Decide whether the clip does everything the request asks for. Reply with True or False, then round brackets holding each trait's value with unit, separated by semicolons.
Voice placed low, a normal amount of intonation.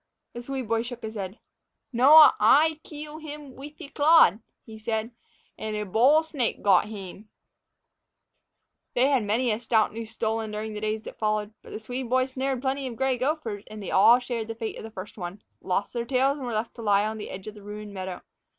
False (225 Hz; 3.8 semitones)